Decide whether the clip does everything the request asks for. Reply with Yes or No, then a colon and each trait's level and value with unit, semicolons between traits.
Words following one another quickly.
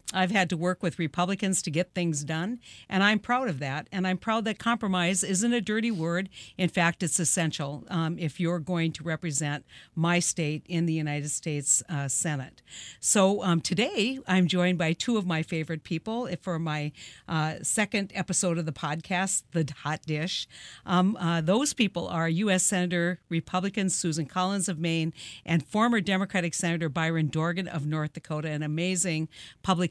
No: average, 175 wpm